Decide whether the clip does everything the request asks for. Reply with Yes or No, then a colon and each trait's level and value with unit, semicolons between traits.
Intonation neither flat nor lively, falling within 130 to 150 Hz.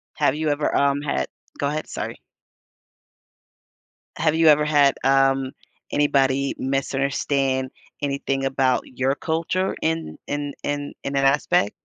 No: narrow, 1.5 semitones; medium, 140 Hz